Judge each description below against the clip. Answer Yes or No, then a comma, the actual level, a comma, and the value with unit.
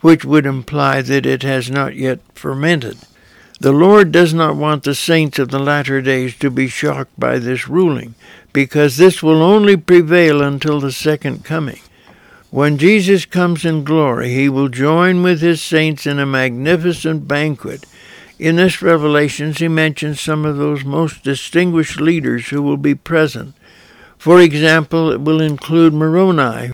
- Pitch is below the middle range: No, medium, 150 Hz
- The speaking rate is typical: Yes, average, 160 wpm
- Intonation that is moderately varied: Yes, average, 3.0 semitones